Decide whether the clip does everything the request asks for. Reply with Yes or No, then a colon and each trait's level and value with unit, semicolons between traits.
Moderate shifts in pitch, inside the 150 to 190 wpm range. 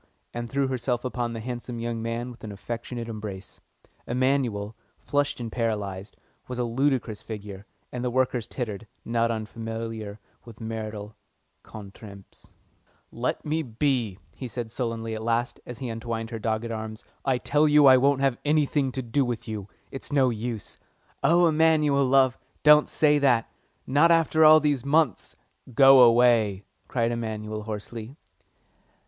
Yes: average, 3.4 semitones; average, 155 wpm